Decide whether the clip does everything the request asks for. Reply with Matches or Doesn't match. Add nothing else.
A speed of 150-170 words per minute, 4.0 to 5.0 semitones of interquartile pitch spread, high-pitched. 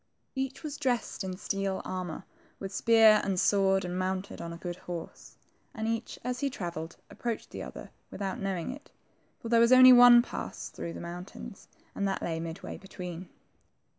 Doesn't match